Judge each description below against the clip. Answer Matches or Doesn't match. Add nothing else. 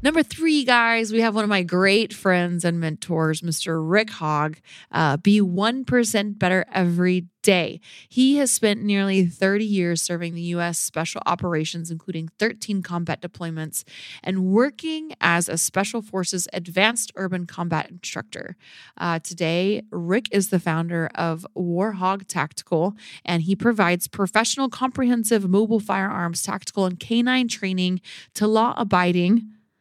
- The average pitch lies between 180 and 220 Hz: Matches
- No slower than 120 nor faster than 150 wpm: Matches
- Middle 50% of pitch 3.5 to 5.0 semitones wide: Matches